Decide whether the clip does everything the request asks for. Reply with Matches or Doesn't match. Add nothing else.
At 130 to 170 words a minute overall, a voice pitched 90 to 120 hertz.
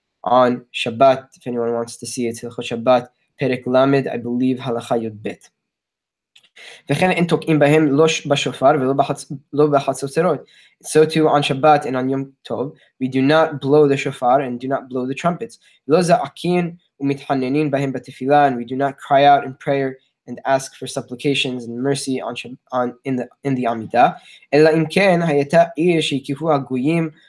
Doesn't match